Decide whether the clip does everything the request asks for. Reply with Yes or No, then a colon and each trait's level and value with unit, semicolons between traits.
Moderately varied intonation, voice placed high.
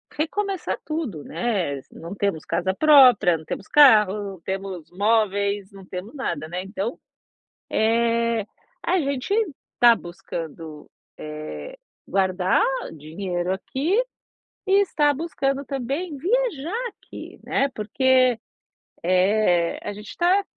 No: wide, 7.2 semitones; high, 215 Hz